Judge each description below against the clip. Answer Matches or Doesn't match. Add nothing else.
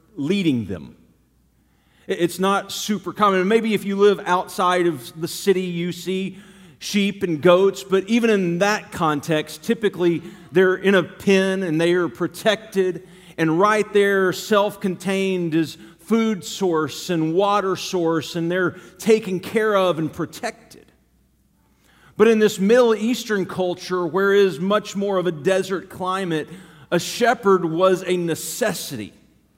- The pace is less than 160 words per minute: Matches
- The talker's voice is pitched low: Doesn't match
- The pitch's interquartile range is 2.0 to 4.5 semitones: Matches